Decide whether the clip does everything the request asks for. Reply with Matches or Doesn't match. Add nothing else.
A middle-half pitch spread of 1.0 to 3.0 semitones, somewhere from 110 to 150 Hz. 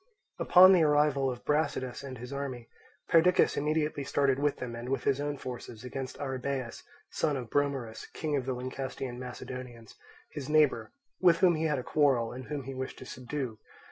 Matches